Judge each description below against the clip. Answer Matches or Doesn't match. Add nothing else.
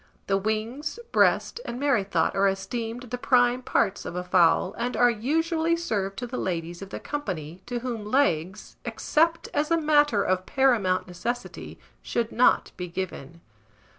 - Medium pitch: Doesn't match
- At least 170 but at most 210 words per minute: Doesn't match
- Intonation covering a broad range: Matches